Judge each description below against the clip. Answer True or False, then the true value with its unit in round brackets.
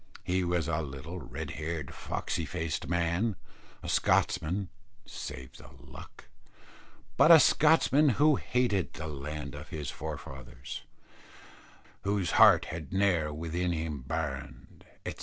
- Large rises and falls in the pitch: False (4.1 semitones)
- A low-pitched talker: True (85 Hz)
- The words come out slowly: True (125 wpm)